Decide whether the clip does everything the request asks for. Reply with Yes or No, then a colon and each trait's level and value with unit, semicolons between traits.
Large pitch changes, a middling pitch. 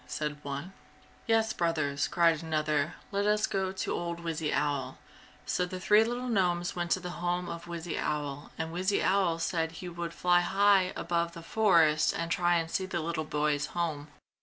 No: average, 2.8 semitones; medium, 170 Hz